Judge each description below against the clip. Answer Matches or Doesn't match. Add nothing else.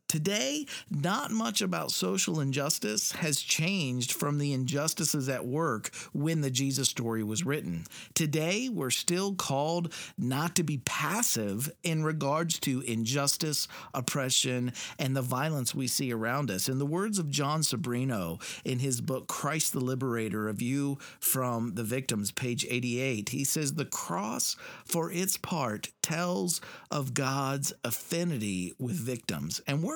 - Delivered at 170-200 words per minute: Doesn't match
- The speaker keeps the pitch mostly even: Doesn't match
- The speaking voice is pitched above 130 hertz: Matches